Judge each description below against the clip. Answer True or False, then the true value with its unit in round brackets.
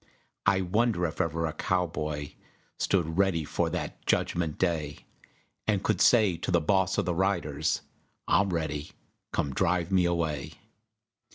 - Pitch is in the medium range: False (85 Hz)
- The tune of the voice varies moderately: True (3.3 semitones)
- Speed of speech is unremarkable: True (145 wpm)